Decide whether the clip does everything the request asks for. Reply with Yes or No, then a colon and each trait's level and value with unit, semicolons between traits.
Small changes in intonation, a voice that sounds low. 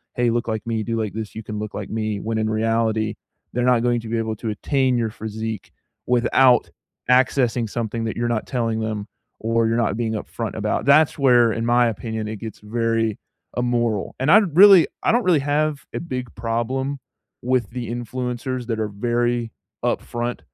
Yes: narrow, 2.0 semitones; low, 115 Hz